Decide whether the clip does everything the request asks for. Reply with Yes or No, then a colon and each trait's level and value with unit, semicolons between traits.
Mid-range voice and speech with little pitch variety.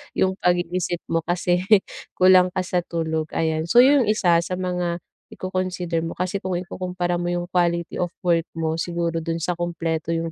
Yes: medium, 175 Hz; narrow, 1.5 semitones